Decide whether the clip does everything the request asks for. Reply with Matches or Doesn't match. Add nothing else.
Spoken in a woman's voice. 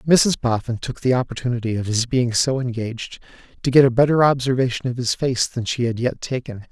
Doesn't match